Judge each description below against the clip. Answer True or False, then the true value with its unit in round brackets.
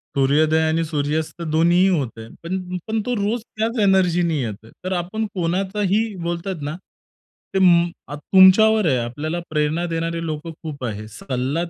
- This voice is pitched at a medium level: True (170 Hz)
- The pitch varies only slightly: False (4.0 semitones)